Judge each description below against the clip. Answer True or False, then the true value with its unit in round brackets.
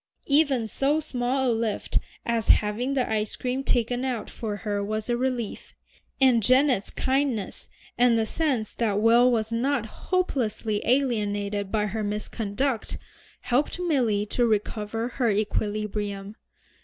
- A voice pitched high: True (230 Hz)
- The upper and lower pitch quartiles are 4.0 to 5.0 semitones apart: False (3.4 semitones)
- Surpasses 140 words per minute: False (135 wpm)